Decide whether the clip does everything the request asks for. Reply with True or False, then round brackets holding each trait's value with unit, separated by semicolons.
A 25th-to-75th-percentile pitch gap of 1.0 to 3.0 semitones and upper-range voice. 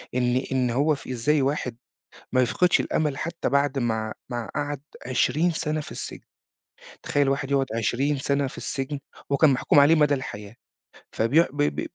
False (2.7 semitones; 140 Hz)